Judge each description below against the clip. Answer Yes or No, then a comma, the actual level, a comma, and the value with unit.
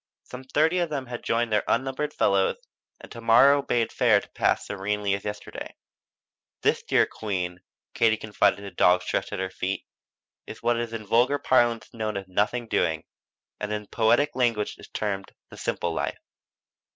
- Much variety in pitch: No, average, 3.4 semitones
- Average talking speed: Yes, average, 175 wpm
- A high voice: No, low, 110 Hz